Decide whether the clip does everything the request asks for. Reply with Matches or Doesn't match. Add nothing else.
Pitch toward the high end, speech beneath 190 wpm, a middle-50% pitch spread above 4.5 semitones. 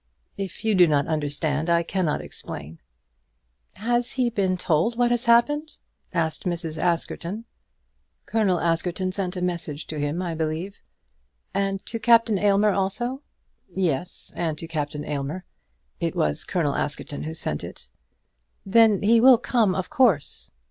Doesn't match